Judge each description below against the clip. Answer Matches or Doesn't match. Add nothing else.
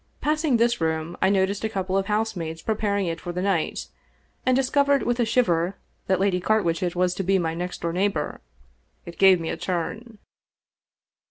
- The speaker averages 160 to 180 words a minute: Matches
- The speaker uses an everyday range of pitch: Matches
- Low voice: Doesn't match